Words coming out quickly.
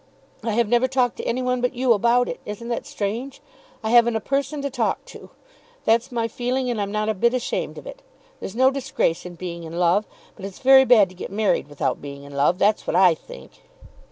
Yes: fast, 230 wpm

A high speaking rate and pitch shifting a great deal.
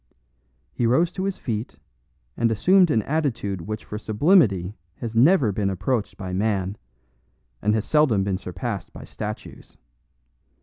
No: average, 140 wpm; wide, 6.0 semitones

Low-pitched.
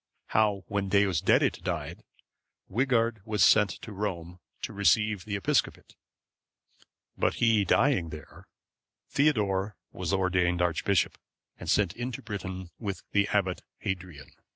Yes: low, 100 Hz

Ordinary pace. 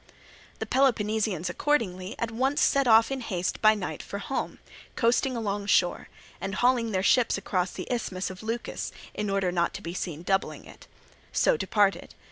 Yes: average, 170 wpm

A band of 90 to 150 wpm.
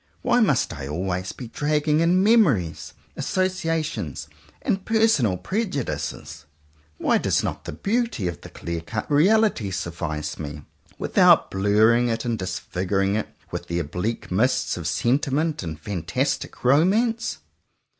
Yes: slow, 135 wpm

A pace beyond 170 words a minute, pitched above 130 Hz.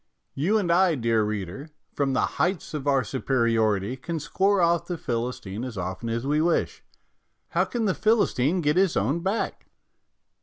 No: average, 165 wpm; medium, 140 Hz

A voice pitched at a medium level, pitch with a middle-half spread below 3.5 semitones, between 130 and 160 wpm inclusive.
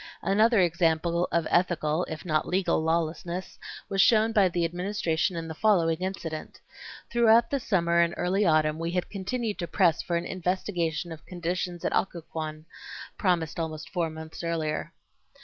Yes: medium, 170 Hz; average, 2.7 semitones; average, 155 wpm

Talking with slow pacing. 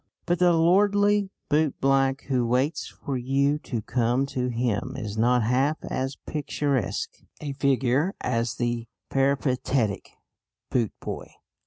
Yes: slow, 120 wpm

